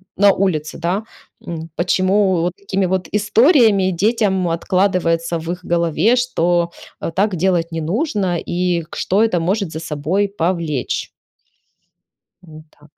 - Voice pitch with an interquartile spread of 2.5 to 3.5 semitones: Yes, average, 3.1 semitones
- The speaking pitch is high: No, medium, 180 Hz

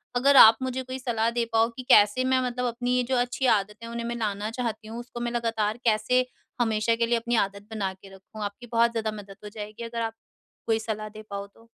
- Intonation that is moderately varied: No, narrow, 2.1 semitones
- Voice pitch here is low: No, high, 230 Hz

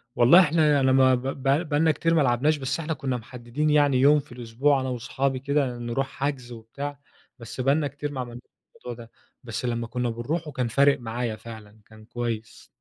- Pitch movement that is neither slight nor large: Yes, average, 3.4 semitones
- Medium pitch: No, low, 130 Hz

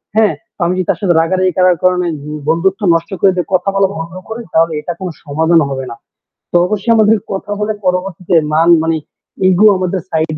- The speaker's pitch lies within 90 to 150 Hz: No, medium, 180 Hz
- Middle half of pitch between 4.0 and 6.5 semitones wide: No, average, 2.8 semitones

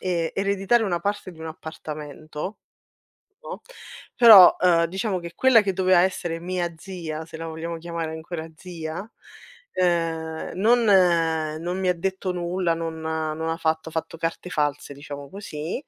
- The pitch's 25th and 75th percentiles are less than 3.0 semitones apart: Yes, narrow, 2.6 semitones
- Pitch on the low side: No, medium, 170 Hz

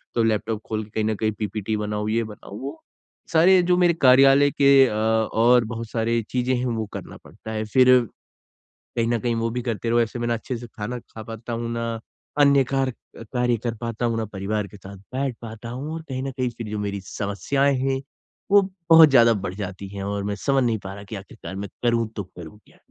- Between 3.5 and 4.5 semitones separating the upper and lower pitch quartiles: No, average, 3.0 semitones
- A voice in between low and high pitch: No, low, 115 Hz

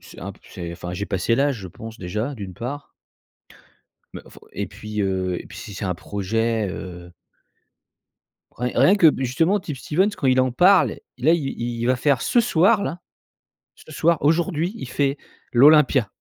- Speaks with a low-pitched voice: Yes, low, 130 Hz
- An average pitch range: No, wide, 7.1 semitones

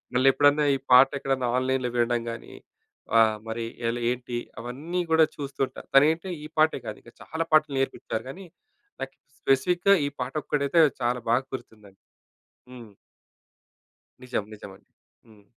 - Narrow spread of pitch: No, average, 3.6 semitones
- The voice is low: Yes, low, 130 Hz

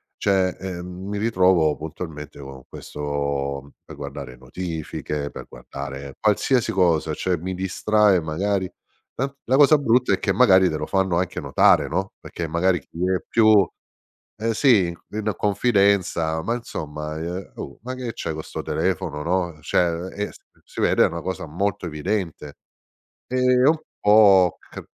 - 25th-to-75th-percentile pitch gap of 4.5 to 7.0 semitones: Yes, average, 4.9 semitones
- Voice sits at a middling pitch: No, very low, 90 Hz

